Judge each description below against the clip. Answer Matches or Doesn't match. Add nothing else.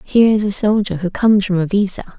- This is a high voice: Matches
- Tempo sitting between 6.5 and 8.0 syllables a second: Matches